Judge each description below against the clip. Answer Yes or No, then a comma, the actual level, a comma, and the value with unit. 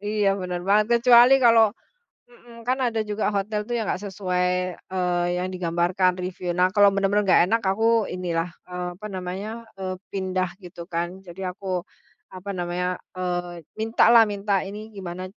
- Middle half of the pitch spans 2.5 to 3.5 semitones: Yes, average, 2.9 semitones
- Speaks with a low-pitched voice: No, high, 190 Hz